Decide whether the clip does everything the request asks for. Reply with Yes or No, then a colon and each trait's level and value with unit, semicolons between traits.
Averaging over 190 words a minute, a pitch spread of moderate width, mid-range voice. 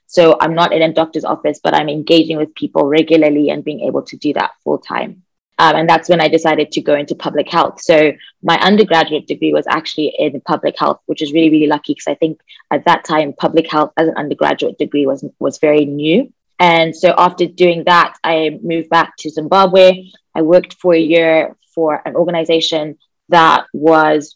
No: average, 200 wpm; narrow, 1.9 semitones; medium, 160 Hz